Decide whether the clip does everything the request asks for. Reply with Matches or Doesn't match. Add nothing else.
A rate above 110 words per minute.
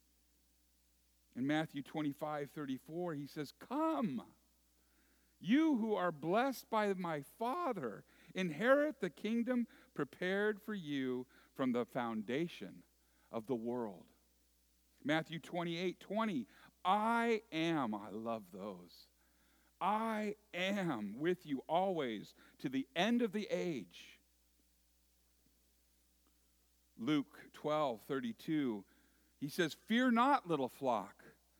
Doesn't match